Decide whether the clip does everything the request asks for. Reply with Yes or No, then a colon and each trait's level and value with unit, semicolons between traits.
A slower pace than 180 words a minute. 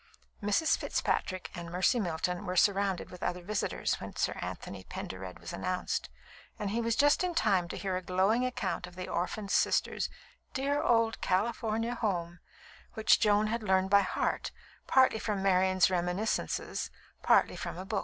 Yes: average, 165 wpm